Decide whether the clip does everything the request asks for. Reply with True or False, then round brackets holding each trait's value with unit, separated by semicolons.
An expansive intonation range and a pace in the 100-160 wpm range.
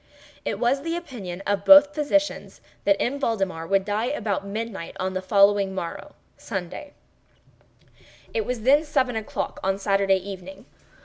True (6.0 semitones; 140 wpm)